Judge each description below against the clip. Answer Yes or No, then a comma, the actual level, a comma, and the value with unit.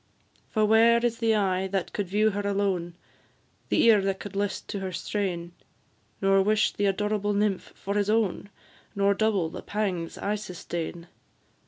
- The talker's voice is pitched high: Yes, high, 200 Hz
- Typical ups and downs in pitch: No, narrow, 1.8 semitones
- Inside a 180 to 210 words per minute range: No, average, 165 wpm